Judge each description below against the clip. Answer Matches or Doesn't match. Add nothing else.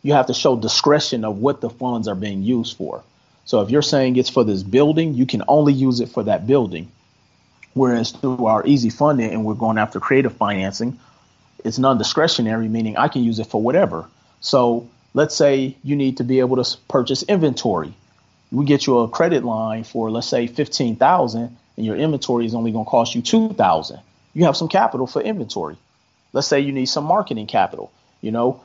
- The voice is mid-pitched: Doesn't match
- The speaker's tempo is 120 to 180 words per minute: Doesn't match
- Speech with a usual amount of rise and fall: Matches